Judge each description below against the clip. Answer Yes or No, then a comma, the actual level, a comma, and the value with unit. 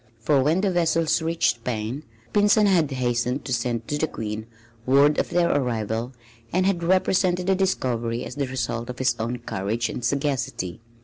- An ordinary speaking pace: Yes, average, 175 wpm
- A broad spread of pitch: Yes, wide, 6.2 semitones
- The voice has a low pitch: Yes, low, 130 Hz